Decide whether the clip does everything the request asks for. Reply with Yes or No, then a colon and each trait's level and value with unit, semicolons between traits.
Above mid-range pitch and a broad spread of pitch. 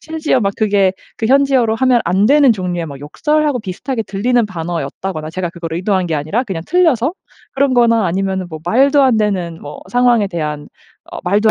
Yes: high, 205 Hz; wide, 6.1 semitones